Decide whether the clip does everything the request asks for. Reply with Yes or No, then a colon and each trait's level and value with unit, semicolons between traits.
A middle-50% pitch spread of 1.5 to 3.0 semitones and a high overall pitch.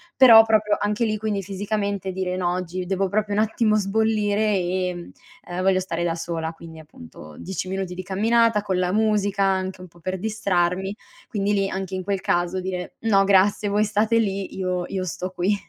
Yes: narrow, 2.4 semitones; high, 195 Hz